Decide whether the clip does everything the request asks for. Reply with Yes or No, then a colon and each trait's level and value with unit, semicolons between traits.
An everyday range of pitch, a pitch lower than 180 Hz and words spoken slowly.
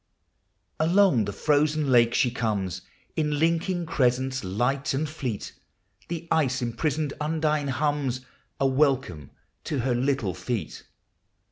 Yes: average, 4.0 semitones; low, 135 Hz; slow, 120 wpm